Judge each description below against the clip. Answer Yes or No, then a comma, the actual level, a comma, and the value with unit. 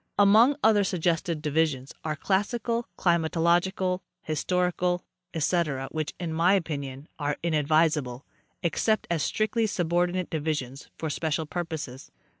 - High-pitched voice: No, medium, 170 Hz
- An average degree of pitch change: Yes, average, 3.0 semitones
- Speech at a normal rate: No, slow, 110 wpm